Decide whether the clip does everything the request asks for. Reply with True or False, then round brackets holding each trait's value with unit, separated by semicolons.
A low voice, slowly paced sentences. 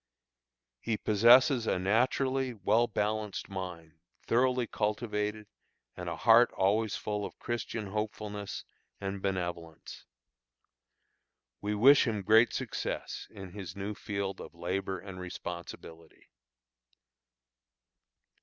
True (105 Hz; 105 wpm)